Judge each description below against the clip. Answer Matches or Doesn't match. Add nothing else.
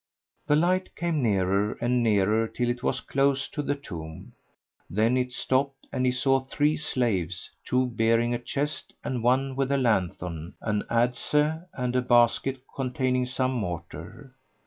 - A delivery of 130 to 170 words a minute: Matches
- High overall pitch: Doesn't match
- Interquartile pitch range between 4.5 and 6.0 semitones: Doesn't match